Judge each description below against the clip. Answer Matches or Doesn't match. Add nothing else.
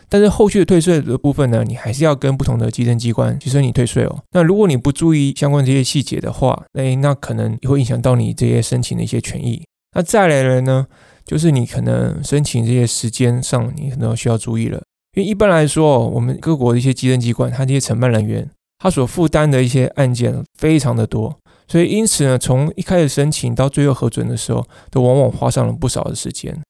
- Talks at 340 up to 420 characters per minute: Matches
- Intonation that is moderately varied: Matches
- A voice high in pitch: Doesn't match